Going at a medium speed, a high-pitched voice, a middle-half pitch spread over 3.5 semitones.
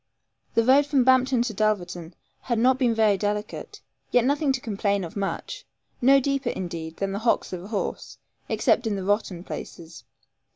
Yes: average, 175 wpm; high, 220 Hz; average, 4.9 semitones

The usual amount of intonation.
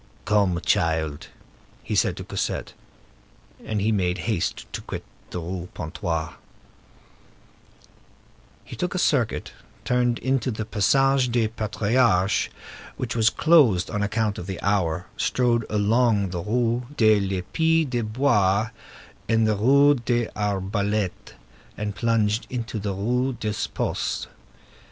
Yes: average, 3.6 semitones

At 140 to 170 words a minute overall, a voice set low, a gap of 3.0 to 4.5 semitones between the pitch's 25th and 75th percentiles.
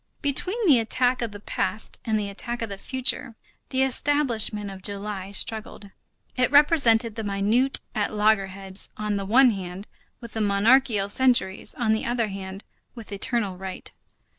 No: average, 160 wpm; high, 220 Hz; average, 3.7 semitones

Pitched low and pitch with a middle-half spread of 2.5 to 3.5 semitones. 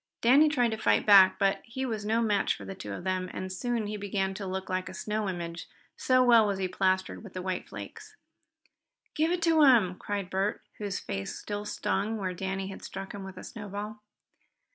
No: high, 200 Hz; average, 3.0 semitones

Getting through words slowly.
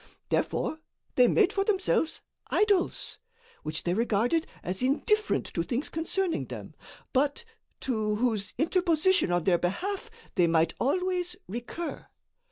Yes: slow, 125 wpm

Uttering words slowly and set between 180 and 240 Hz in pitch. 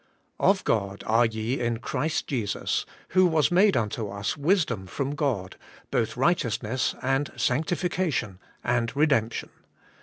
No: slow, 125 wpm; low, 125 Hz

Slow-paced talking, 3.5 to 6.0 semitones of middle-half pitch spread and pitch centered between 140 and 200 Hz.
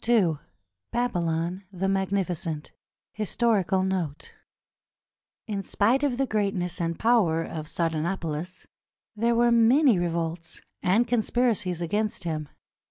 Yes: slow, 105 wpm; average, 5.1 semitones; high, 190 Hz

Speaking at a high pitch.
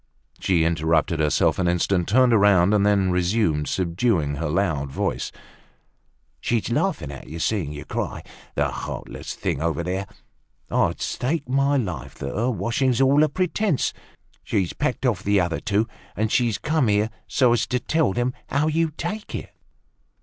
No: low, 105 Hz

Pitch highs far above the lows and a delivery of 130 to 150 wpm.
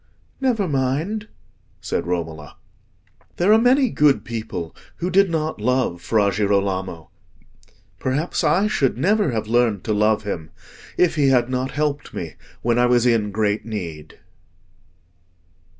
Yes: wide, 7.3 semitones; slow, 135 wpm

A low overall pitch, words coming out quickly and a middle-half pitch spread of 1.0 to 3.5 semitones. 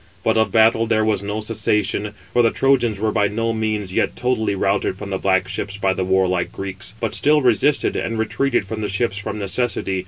Yes: low, 105 Hz; fast, 210 wpm; narrow, 2.6 semitones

